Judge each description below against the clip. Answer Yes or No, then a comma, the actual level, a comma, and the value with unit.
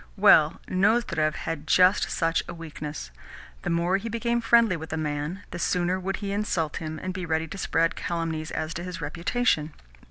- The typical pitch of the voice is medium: Yes, medium, 170 Hz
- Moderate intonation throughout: Yes, average, 3.4 semitones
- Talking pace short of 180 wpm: No, average, 185 wpm